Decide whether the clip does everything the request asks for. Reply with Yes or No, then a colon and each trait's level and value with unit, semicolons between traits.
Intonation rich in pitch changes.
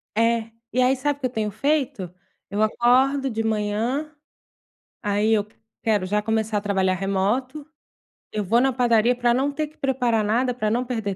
No: average, 3.5 semitones